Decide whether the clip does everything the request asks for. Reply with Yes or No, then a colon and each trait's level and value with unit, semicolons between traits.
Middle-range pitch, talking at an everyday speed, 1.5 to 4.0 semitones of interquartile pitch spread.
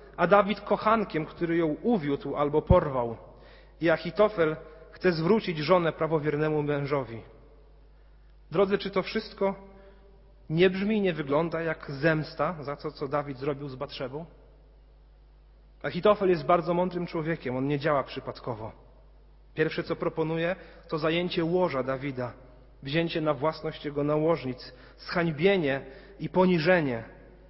Yes: medium, 160 Hz; average, 125 wpm; average, 3.7 semitones